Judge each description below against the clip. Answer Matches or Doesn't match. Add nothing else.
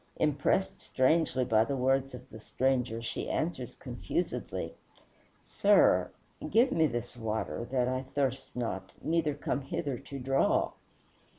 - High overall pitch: Doesn't match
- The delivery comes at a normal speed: Doesn't match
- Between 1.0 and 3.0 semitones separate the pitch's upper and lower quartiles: Matches